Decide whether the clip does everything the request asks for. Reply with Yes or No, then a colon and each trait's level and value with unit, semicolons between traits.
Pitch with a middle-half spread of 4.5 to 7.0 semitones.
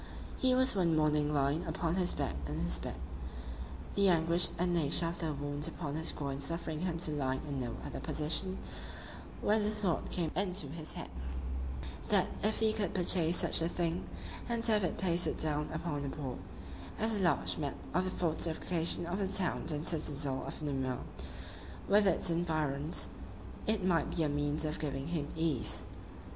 No: average, 3.6 semitones